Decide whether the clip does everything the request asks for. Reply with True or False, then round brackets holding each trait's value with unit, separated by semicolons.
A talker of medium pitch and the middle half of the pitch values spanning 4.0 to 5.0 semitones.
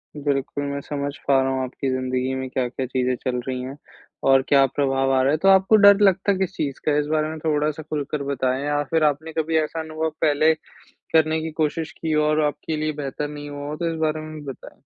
False (145 Hz; 2.8 semitones)